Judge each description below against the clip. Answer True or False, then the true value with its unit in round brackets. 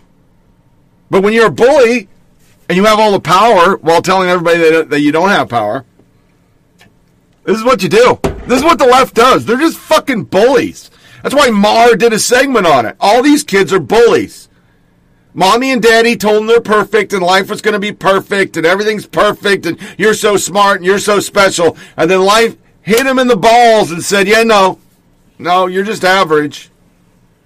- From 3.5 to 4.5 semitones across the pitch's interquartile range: True (3.8 semitones)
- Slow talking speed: False (195 wpm)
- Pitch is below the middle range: False (205 Hz)